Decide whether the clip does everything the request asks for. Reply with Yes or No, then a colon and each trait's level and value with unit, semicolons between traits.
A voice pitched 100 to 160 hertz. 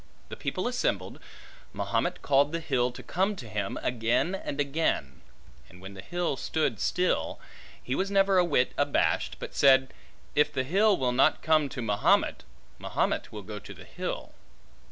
Yes: medium, 140 Hz